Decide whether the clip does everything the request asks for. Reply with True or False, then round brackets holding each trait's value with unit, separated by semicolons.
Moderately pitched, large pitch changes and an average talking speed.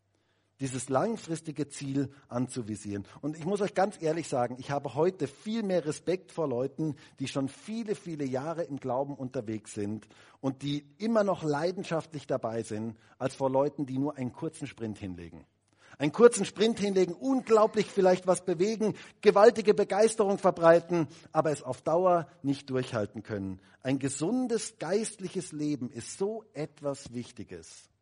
True (145 Hz; 6.3 semitones; 150 wpm)